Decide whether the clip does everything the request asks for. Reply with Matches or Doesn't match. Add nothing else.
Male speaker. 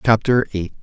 Matches